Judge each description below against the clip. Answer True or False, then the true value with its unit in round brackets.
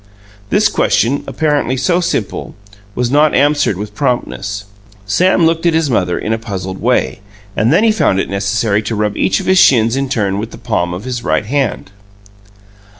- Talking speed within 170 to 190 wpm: True (185 wpm)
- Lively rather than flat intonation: True (6.3 semitones)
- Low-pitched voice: True (120 Hz)